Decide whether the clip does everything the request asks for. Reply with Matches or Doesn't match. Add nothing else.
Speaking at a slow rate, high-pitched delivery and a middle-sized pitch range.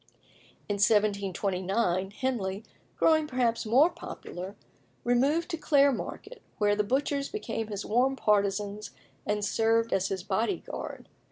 Matches